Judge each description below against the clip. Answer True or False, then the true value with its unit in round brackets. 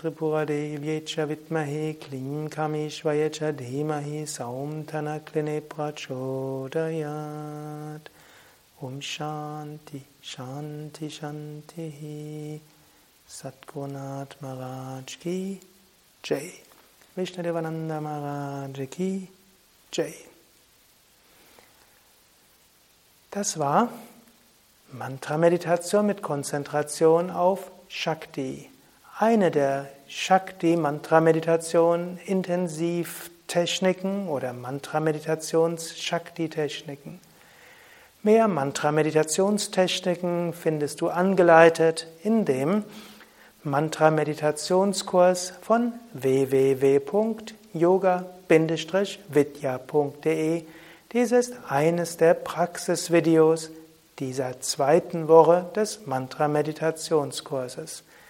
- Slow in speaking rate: True (65 wpm)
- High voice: False (160 Hz)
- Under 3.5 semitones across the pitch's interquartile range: True (3.0 semitones)